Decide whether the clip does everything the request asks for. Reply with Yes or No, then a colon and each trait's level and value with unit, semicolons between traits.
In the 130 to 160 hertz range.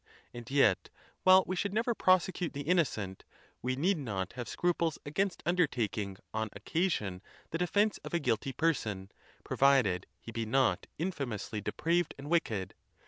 Yes: medium, 140 Hz